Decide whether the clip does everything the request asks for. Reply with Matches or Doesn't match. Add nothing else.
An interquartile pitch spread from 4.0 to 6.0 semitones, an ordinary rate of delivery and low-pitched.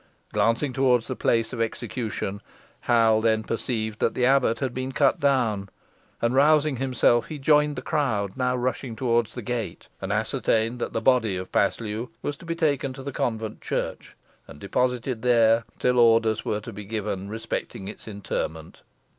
Doesn't match